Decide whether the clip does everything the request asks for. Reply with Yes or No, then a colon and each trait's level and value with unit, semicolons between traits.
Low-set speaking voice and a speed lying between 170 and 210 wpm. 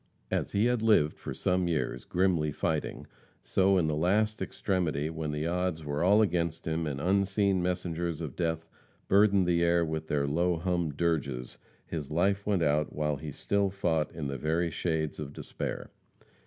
Yes: very low, 85 Hz; average, 175 wpm